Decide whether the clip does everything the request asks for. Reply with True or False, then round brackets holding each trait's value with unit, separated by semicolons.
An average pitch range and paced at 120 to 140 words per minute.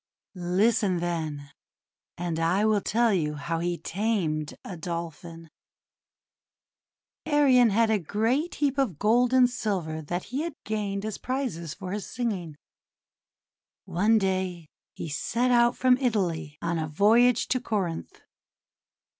False (5.9 semitones; 135 wpm)